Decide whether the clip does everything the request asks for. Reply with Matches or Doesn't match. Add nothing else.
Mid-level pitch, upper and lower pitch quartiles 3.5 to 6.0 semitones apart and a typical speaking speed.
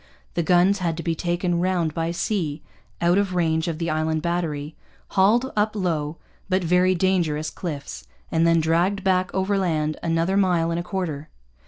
Doesn't match